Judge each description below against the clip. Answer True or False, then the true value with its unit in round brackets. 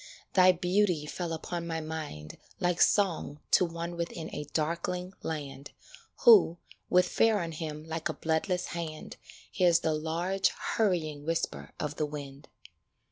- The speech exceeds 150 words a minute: False (140 wpm)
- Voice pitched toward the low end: False (165 Hz)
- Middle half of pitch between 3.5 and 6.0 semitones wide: False (2.7 semitones)